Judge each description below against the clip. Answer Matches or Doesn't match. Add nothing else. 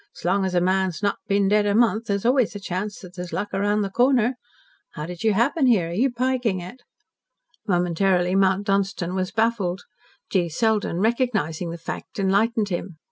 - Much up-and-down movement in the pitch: Doesn't match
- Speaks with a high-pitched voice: Matches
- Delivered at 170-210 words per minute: Matches